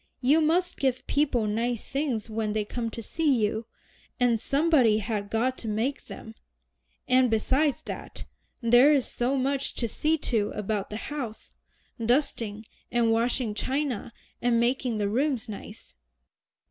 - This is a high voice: Yes, high, 240 Hz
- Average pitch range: Yes, average, 3.8 semitones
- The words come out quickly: No, average, 145 wpm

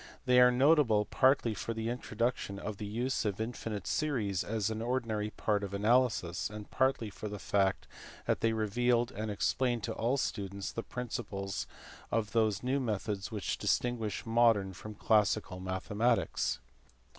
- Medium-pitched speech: No, low, 110 Hz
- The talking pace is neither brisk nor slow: Yes, average, 155 wpm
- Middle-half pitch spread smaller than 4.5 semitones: Yes, average, 3.1 semitones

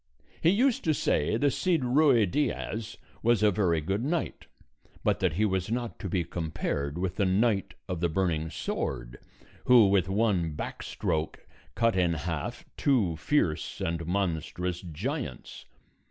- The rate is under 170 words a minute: Yes, average, 155 wpm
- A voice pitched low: Yes, very low, 95 Hz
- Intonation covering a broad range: Yes, wide, 6.0 semitones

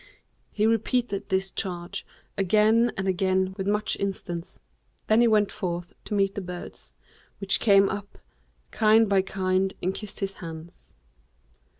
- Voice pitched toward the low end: No, high, 195 Hz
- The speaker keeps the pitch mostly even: Yes, narrow, 2.0 semitones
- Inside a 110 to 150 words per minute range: Yes, average, 140 wpm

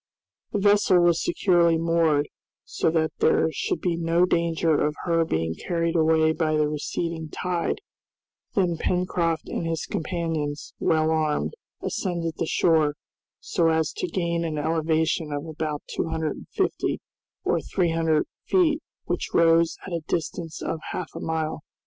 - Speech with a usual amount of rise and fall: No, narrow, 1.4 semitones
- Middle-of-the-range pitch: Yes, medium, 165 Hz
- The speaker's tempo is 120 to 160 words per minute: Yes, average, 155 wpm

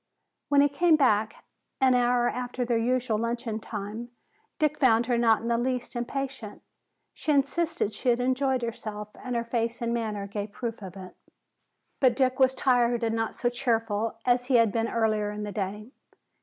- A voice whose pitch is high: Yes, high, 235 Hz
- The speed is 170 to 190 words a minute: Yes, average, 185 wpm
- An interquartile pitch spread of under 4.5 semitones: Yes, narrow, 2.6 semitones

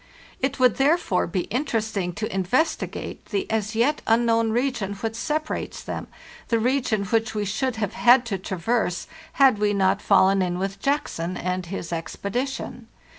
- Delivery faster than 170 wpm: No, average, 155 wpm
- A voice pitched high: Yes, high, 220 Hz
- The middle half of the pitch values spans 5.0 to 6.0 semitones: No, average, 4.3 semitones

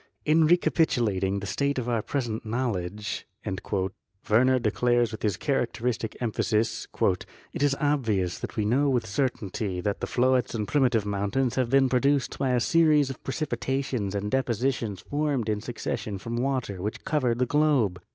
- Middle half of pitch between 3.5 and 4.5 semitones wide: Yes, average, 4.1 semitones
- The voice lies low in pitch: Yes, low, 120 Hz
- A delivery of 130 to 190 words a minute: Yes, average, 160 wpm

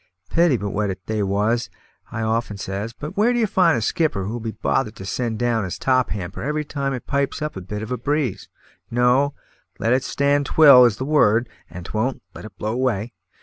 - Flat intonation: No, average, 4.8 semitones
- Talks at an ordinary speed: No, fast, 220 wpm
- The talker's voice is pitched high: No, low, 120 Hz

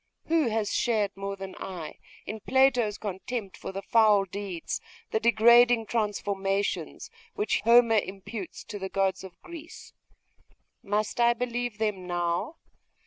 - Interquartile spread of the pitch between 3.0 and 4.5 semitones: Yes, average, 3.5 semitones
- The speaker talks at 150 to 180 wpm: No, slow, 135 wpm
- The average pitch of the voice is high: Yes, high, 210 Hz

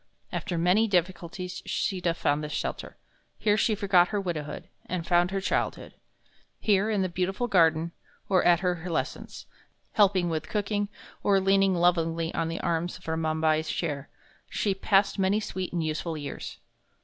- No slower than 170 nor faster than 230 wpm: No, average, 155 wpm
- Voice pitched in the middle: Yes, medium, 180 Hz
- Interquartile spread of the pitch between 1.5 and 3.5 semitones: Yes, average, 2.9 semitones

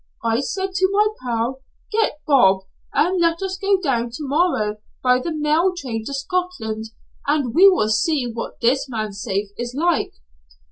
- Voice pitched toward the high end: Yes, very high, 275 Hz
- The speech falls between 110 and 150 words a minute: No, average, 170 wpm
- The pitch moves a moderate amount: No, wide, 7.5 semitones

